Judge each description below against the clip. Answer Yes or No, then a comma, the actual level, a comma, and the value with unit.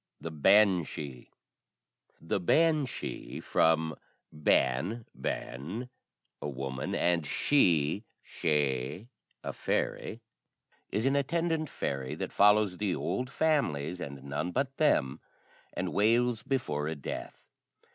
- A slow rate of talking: Yes, slow, 105 wpm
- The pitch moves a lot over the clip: Yes, wide, 9.0 semitones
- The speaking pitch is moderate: No, very low, 90 Hz